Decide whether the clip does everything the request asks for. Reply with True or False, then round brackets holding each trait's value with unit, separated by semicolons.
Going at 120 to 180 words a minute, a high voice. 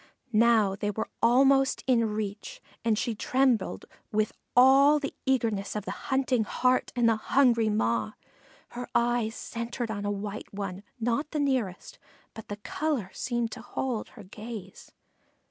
True (155 wpm; 230 Hz)